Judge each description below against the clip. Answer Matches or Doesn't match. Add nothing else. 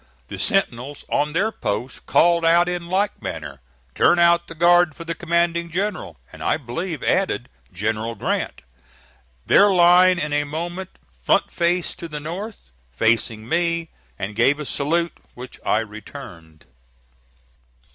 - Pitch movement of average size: Doesn't match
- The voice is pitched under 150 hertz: Doesn't match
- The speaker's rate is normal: Matches